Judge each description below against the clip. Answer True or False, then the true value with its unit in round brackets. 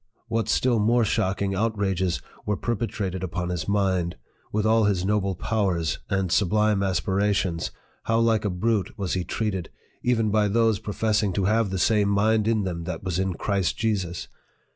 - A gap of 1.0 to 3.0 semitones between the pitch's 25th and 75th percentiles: True (2.7 semitones)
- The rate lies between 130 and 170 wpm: True (165 wpm)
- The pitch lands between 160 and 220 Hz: False (100 Hz)